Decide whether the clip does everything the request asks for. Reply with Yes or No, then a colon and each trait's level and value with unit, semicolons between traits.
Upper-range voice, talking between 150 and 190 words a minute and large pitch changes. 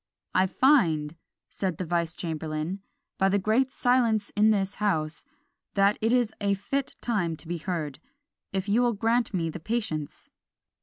No: high, 195 Hz; average, 160 wpm; average, 5.0 semitones